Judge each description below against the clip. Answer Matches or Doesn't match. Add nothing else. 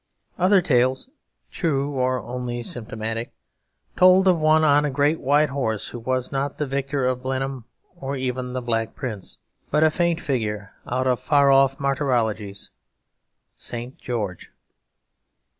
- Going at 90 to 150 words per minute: Matches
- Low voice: Matches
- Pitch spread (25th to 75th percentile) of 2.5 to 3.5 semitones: Matches